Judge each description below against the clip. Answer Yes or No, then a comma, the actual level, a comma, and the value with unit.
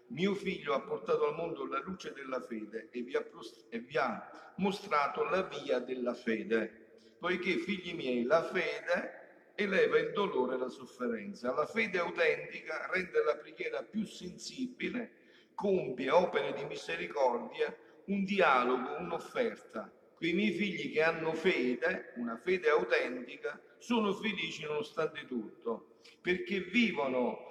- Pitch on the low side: No, high, 190 Hz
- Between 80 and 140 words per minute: Yes, average, 130 wpm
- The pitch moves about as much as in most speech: No, wide, 8.0 semitones